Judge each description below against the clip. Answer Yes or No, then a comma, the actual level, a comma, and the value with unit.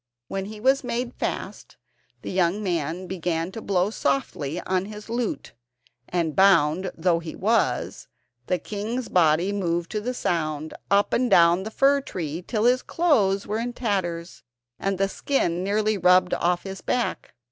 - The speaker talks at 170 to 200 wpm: No, average, 160 wpm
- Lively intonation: No, average, 4.1 semitones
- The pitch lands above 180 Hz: Yes, high, 190 Hz